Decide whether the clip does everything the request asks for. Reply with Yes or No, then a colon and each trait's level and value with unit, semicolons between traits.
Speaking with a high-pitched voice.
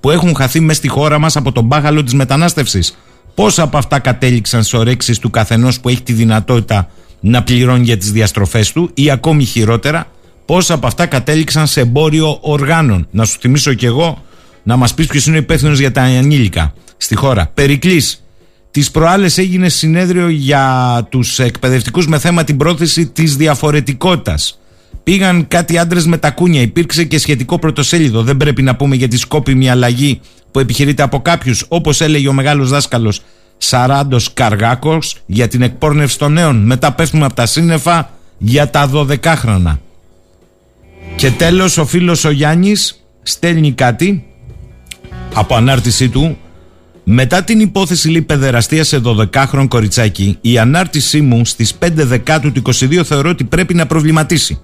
No: medium, 140 Hz